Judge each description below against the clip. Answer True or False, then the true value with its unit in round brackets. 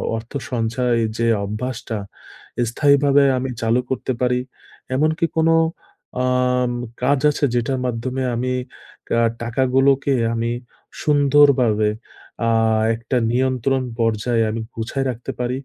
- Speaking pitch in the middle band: False (125 Hz)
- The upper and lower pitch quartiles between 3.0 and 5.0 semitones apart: False (2.6 semitones)